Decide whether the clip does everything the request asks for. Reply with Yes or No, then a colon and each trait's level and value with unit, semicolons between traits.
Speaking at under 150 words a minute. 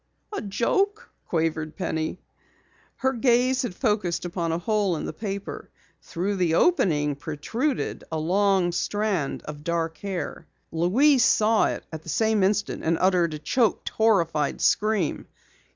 Yes: average, 140 wpm